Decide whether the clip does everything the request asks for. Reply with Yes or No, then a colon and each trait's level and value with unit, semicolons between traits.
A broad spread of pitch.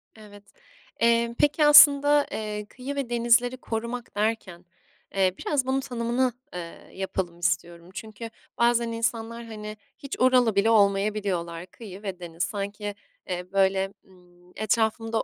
No: average, 3.6 semitones